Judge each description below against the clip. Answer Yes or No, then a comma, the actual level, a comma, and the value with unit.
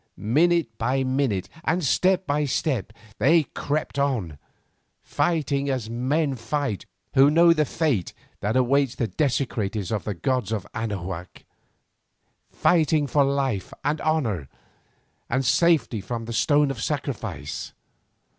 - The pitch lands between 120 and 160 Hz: Yes, low, 135 Hz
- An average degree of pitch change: Yes, average, 5.0 semitones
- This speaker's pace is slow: Yes, slow, 125 wpm